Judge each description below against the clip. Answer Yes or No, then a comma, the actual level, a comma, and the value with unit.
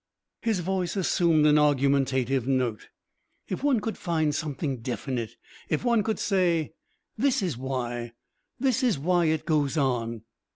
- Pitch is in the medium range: Yes, medium, 150 Hz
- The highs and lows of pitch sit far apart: Yes, wide, 5.9 semitones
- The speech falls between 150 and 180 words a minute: No, average, 140 wpm